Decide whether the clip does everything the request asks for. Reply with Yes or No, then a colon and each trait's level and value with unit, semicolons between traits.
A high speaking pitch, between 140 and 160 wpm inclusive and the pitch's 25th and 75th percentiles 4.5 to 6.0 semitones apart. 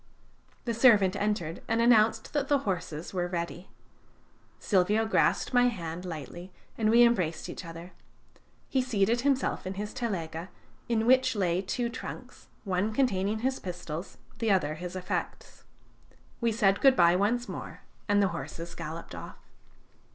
Yes: high, 200 Hz; average, 150 wpm; average, 4.9 semitones